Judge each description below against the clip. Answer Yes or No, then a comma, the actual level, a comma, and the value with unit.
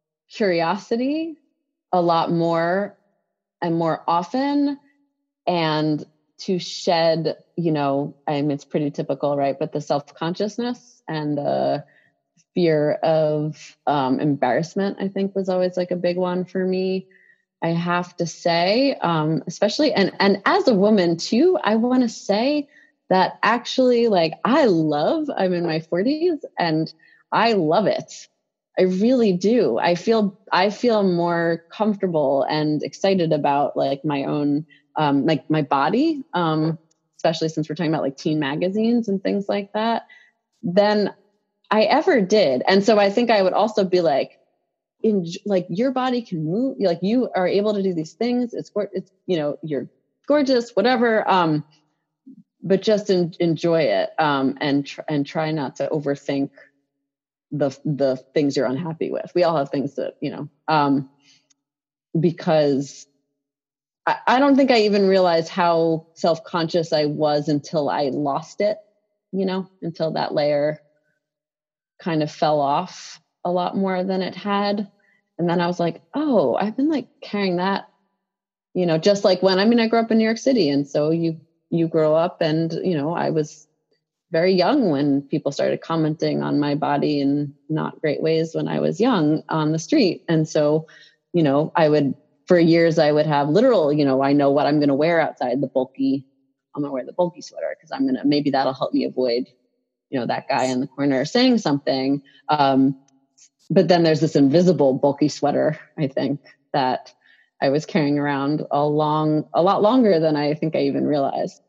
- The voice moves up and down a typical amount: Yes, average, 5.0 semitones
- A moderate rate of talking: Yes, average, 175 wpm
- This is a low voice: No, medium, 165 Hz